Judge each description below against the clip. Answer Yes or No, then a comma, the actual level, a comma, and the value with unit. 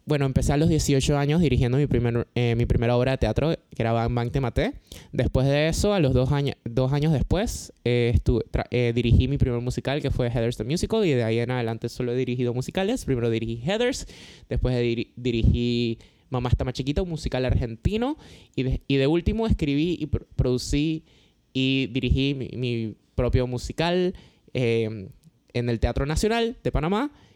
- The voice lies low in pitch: Yes, low, 125 Hz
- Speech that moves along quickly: Yes, fast, 195 wpm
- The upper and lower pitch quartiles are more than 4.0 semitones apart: No, average, 3.3 semitones